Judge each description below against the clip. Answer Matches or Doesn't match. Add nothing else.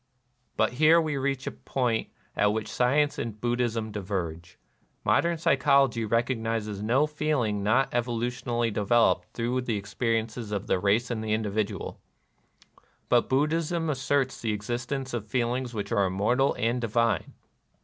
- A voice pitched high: Doesn't match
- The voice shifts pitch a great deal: Doesn't match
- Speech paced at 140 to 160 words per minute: Matches